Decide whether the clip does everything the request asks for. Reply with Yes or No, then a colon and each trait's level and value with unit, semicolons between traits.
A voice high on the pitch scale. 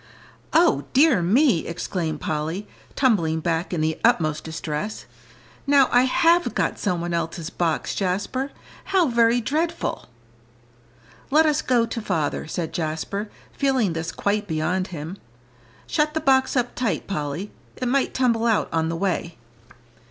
Yes: high, 200 Hz